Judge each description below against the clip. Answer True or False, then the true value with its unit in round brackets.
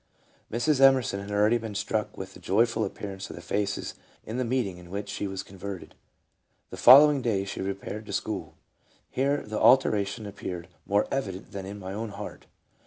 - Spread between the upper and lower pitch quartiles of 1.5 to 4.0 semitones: True (3.3 semitones)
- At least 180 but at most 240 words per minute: True (185 wpm)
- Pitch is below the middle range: True (105 Hz)